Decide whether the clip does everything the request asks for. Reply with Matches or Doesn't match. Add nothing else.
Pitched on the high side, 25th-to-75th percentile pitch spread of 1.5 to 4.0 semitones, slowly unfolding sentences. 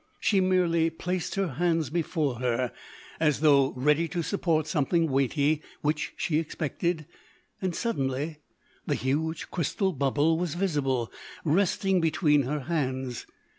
Doesn't match